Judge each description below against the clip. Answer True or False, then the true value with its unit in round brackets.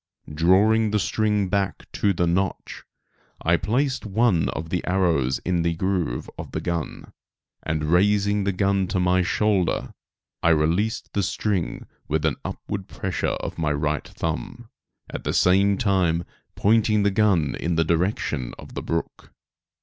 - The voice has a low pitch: True (95 Hz)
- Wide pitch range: False (3.6 semitones)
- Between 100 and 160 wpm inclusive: True (155 wpm)